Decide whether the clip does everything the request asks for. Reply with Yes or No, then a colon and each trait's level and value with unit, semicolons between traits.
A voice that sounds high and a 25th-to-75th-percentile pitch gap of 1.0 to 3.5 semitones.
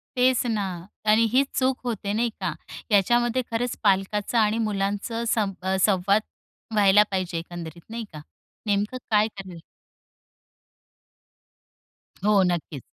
Yes: high, 210 Hz; average, 3.1 semitones